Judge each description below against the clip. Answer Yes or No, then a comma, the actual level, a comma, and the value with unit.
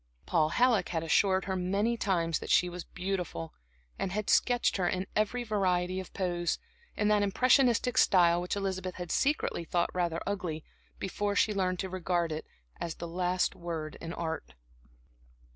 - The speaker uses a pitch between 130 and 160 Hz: No, medium, 185 Hz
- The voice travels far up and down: No, average, 2.8 semitones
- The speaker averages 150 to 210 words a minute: Yes, average, 165 wpm